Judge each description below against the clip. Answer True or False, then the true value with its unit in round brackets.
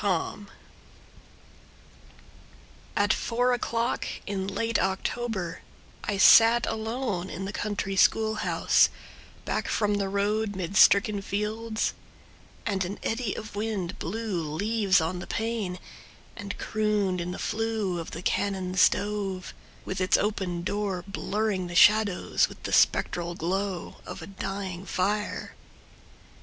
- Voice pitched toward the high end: True (200 Hz)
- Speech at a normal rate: False (130 wpm)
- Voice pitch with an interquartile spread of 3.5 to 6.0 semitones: False (2.8 semitones)